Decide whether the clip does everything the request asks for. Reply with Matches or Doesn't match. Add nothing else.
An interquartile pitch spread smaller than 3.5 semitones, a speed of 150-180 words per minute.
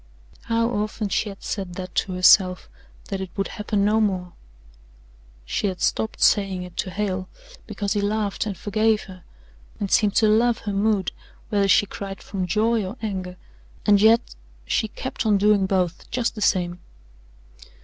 Matches